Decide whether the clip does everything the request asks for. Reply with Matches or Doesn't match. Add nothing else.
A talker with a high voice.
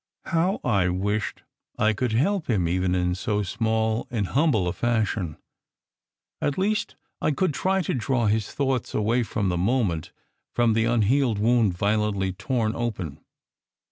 Doesn't match